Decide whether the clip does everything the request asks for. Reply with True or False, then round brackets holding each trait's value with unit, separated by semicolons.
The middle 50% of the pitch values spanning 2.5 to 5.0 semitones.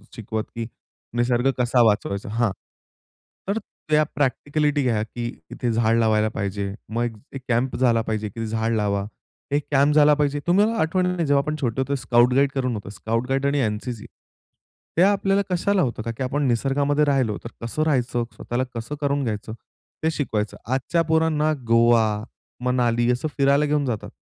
True (4.2 semitones)